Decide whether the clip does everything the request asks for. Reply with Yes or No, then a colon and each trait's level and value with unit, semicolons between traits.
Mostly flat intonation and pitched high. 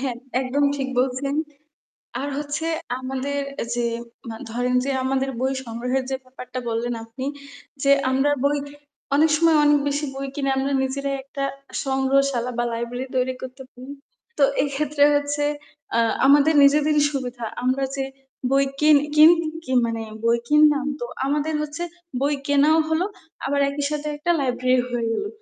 Yes: narrow, 2.3 semitones; very high, 275 Hz